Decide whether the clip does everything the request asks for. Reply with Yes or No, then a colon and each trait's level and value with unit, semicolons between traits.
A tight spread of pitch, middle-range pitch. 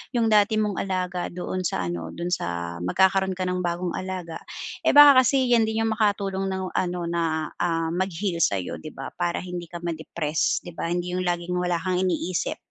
Yes: narrow, 2.2 semitones; medium, 180 Hz